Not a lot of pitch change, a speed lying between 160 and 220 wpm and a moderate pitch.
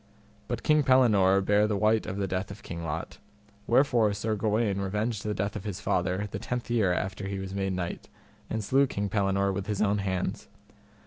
No: narrow, 2.2 semitones; average, 200 wpm; low, 100 Hz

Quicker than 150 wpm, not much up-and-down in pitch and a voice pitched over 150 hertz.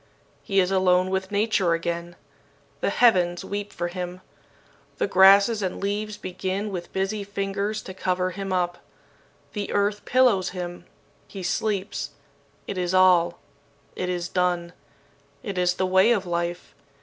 No: average, 145 wpm; narrow, 2.1 semitones; medium, 185 Hz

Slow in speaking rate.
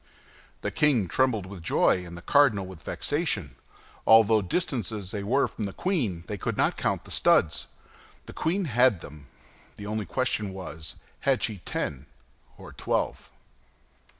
No: average, 155 wpm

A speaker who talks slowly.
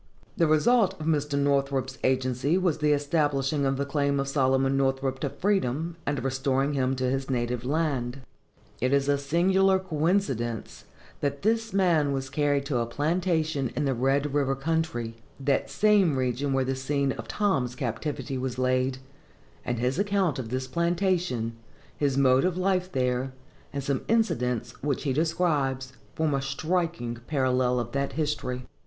No: average, 160 wpm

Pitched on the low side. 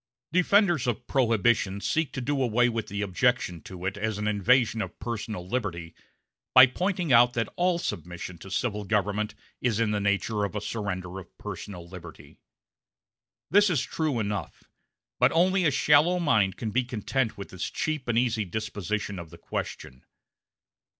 Yes: low, 110 Hz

